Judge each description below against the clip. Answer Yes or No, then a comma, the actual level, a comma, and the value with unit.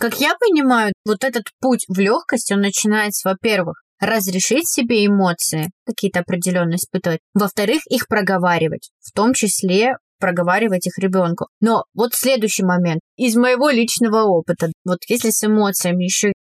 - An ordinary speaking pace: Yes, average, 140 wpm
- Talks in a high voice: Yes, high, 205 Hz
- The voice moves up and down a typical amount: Yes, average, 4.2 semitones